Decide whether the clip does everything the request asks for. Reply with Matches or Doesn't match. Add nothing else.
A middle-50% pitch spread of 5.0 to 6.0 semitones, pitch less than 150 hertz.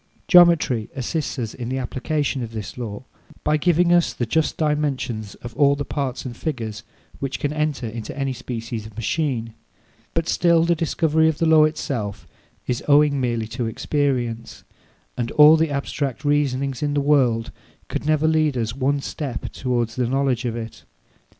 Doesn't match